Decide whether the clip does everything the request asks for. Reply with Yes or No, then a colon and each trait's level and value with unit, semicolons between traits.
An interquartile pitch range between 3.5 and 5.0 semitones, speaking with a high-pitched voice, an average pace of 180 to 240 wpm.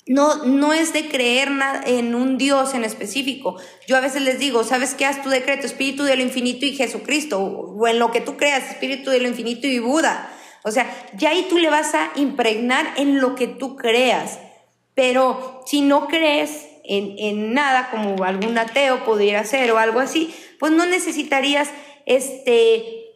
No: average, 3.0 semitones; very high, 265 Hz; average, 185 wpm